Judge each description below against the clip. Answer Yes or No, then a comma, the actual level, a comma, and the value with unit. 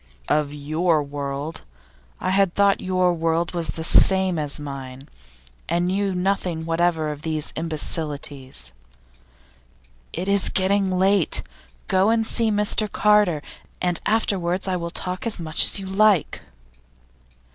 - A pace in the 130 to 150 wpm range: Yes, slow, 135 wpm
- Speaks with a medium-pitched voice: Yes, medium, 175 Hz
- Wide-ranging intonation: No, average, 3.8 semitones